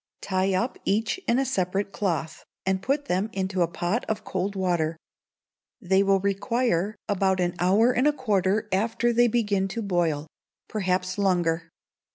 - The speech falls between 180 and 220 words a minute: No, average, 160 wpm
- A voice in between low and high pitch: No, high, 195 Hz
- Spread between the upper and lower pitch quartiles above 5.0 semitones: No, average, 3.2 semitones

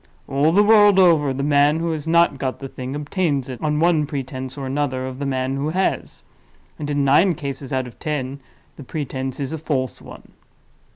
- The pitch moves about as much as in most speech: Yes, average, 3.0 semitones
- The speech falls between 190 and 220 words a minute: Yes, average, 195 wpm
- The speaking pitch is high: No, medium, 145 Hz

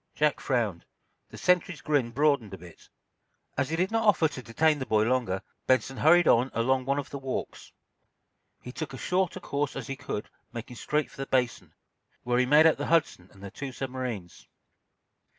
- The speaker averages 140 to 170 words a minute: No, average, 195 wpm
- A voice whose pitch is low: Yes, low, 130 Hz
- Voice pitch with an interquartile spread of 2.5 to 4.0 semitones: No, average, 4.4 semitones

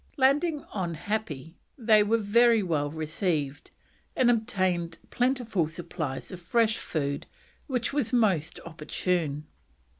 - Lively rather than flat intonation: Yes, wide, 6.5 semitones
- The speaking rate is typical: No, slow, 115 wpm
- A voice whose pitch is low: No, medium, 185 Hz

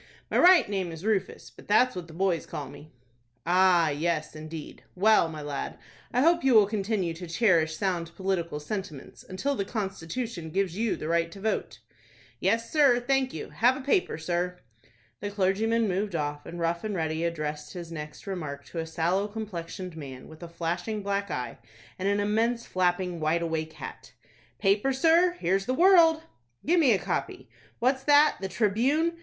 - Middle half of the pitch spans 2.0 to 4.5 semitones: No, average, 5.2 semitones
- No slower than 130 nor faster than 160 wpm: No, average, 175 wpm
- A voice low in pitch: No, high, 190 Hz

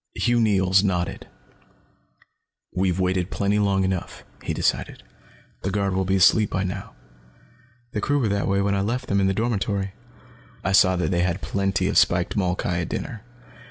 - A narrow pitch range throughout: Yes, narrow, 1.6 semitones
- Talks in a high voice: No, very low, 95 Hz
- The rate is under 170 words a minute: No, average, 175 wpm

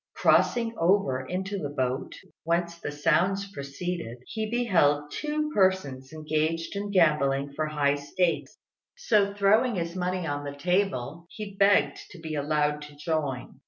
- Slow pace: No, average, 145 wpm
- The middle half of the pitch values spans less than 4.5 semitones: No, average, 5.2 semitones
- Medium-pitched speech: Yes, medium, 165 Hz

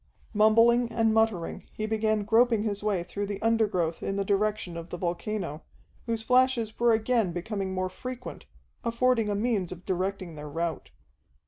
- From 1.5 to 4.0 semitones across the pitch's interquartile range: Yes, average, 3.6 semitones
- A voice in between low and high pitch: No, high, 210 Hz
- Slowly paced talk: No, average, 160 wpm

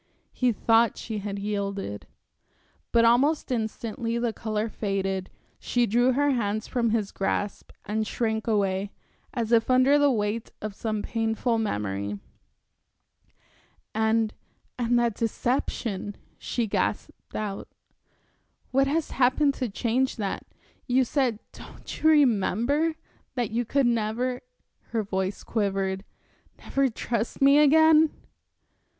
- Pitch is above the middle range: Yes, high, 230 Hz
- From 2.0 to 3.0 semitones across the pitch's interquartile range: No, average, 3.5 semitones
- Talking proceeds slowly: Yes, slow, 120 wpm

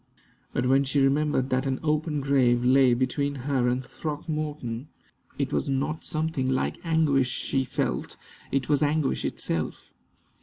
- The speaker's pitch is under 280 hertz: Yes, low, 135 Hz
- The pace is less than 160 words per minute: Yes, average, 145 wpm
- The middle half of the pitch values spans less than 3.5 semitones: Yes, narrow, 2.6 semitones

